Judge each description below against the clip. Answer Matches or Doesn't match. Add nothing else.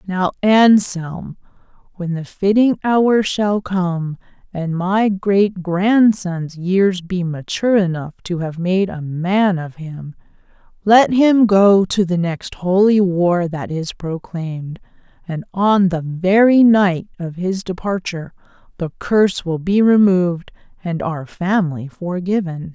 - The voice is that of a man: Doesn't match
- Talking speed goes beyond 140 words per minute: Doesn't match